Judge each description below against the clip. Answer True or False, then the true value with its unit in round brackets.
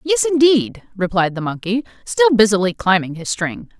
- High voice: True (220 Hz)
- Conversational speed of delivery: True (175 wpm)